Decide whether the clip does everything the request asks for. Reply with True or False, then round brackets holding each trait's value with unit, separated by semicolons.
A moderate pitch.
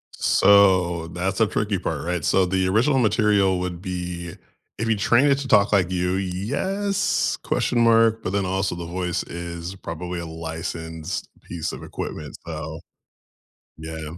False (90 Hz)